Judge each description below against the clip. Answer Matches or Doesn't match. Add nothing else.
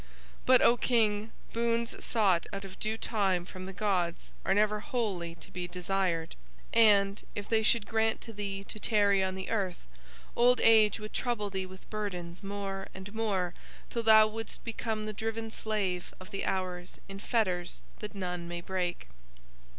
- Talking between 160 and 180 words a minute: Matches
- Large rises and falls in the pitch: Doesn't match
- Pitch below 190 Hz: Doesn't match